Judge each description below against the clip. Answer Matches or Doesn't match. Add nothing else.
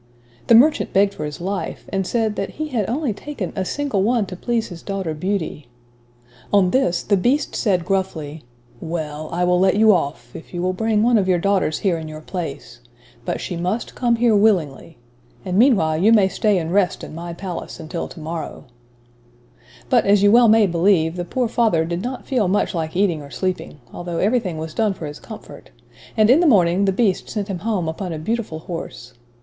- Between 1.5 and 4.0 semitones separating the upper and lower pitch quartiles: Doesn't match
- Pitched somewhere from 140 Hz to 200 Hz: Matches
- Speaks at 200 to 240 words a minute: Matches